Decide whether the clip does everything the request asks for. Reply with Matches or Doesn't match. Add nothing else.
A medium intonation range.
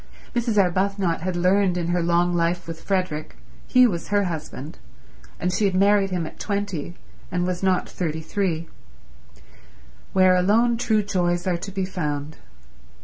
Matches